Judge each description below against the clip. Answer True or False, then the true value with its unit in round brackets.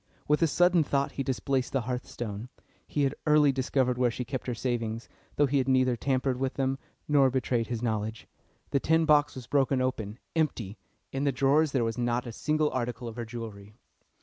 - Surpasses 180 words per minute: True (200 wpm)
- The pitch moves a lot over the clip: False (2.8 semitones)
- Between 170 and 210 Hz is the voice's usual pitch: False (130 Hz)